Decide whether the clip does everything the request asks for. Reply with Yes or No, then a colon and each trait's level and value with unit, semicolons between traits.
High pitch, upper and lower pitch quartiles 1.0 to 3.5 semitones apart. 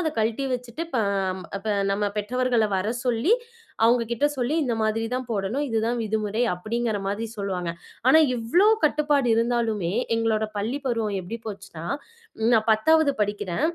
Yes: high, 225 Hz; average, 3.0 semitones